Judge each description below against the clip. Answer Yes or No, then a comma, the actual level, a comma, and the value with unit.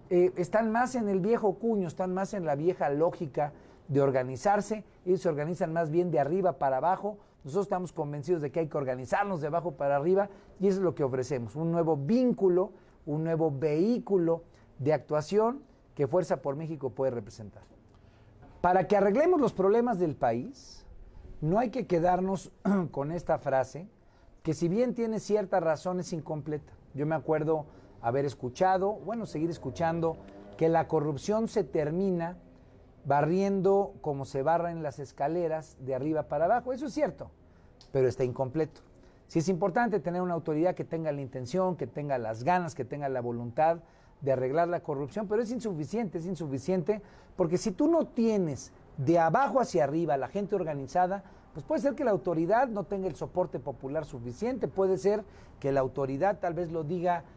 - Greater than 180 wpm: No, average, 175 wpm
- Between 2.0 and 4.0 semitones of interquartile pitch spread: No, wide, 5.5 semitones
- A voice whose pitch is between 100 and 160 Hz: No, medium, 170 Hz